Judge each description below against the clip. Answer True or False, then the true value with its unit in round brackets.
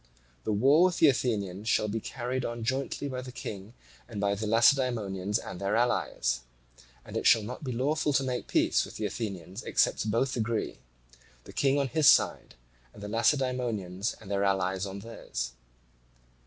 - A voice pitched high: False (115 Hz)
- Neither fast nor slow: True (175 wpm)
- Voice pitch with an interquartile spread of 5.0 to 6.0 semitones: False (4.2 semitones)